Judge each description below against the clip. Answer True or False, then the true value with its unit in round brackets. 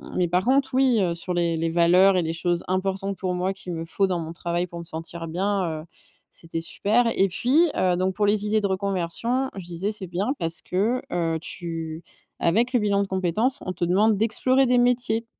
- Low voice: False (185 Hz)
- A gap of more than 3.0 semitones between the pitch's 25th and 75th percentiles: True (3.7 semitones)